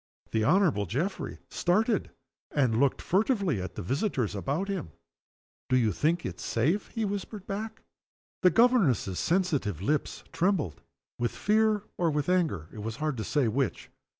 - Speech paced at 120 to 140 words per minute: No, average, 150 wpm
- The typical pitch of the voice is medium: Yes, medium, 155 Hz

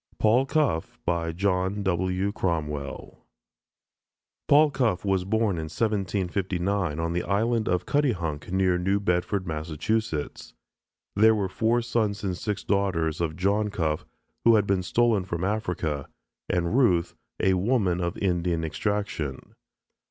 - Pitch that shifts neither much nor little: Yes, average, 3.6 semitones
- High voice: No, very low, 95 Hz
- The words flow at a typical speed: No, slow, 130 wpm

